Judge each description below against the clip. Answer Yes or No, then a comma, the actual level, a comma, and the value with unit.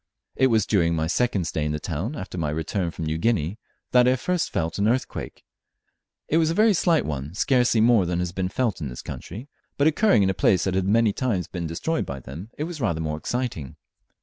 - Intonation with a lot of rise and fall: Yes, wide, 7.4 semitones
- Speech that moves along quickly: Yes, fast, 230 wpm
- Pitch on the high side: No, very low, 95 Hz